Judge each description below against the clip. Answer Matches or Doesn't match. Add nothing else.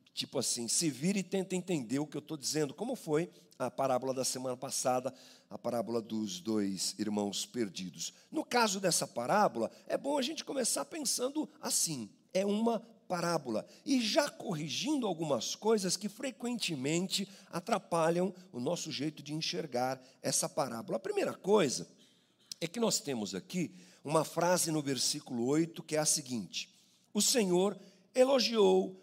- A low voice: Doesn't match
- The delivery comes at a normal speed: Matches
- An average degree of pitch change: Doesn't match